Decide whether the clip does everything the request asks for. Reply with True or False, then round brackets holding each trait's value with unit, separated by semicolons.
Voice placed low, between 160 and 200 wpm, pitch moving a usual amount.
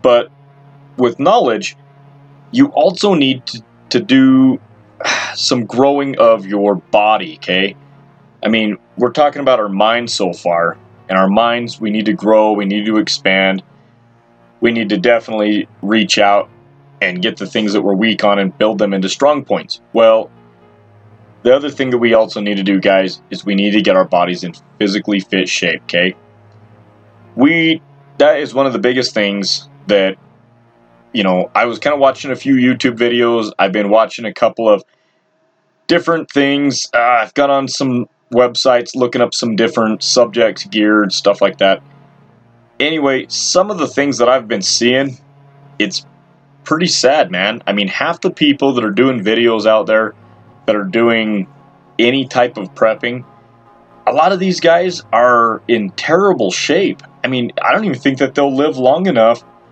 True (120 Hz; 175 wpm; 4.9 semitones)